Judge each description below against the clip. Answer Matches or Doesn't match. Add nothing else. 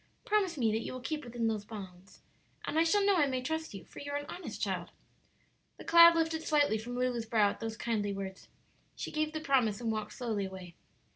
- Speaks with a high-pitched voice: Matches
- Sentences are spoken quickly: Matches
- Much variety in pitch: Matches